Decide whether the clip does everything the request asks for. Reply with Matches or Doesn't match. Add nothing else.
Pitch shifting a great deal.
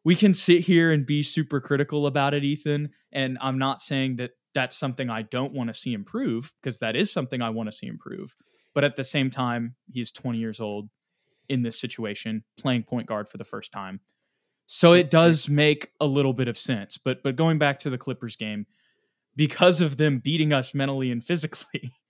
Doesn't match